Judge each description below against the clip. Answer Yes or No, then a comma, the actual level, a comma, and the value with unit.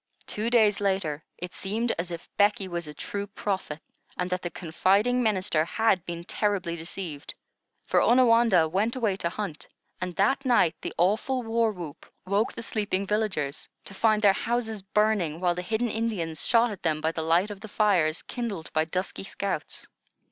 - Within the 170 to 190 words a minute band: Yes, average, 175 wpm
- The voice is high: Yes, high, 195 Hz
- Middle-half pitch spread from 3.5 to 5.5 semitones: Yes, average, 4.2 semitones